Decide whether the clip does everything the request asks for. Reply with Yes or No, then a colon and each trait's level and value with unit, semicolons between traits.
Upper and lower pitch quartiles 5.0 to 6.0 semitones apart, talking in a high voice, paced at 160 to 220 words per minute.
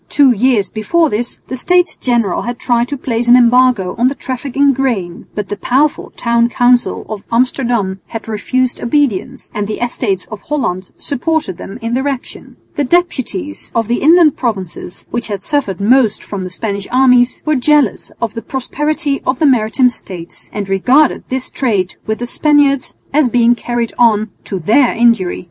No: average, 4.1 semitones; high, 240 Hz; average, 175 wpm